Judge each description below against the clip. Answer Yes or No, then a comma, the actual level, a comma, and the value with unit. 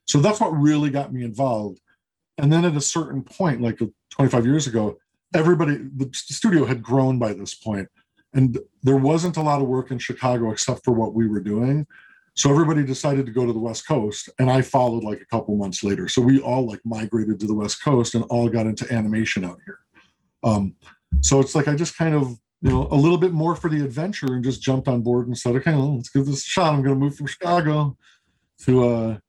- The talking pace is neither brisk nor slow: No, fast, 230 wpm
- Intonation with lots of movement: No, average, 4.2 semitones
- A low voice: Yes, low, 130 Hz